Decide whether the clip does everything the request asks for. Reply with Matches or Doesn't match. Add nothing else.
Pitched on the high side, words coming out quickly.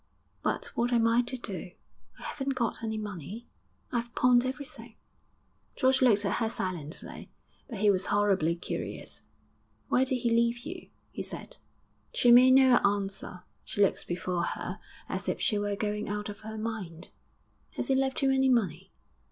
Doesn't match